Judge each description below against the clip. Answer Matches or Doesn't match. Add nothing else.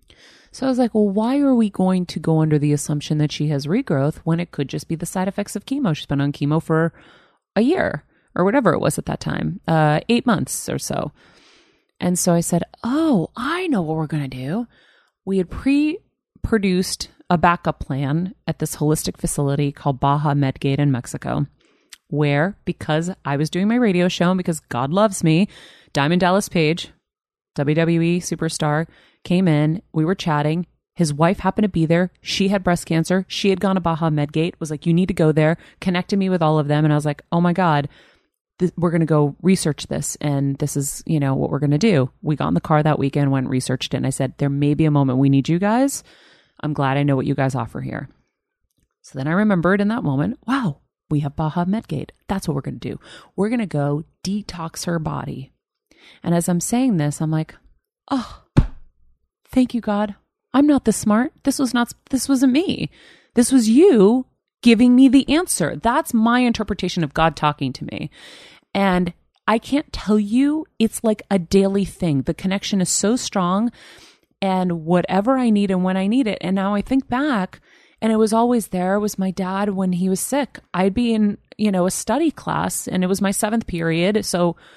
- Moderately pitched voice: Matches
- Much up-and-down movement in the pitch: Matches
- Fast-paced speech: Matches